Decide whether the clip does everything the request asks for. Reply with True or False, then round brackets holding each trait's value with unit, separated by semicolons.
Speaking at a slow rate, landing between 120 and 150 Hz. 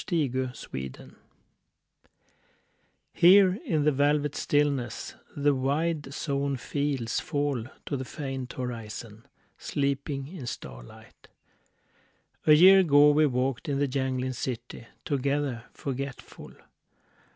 True (105 wpm; 140 Hz)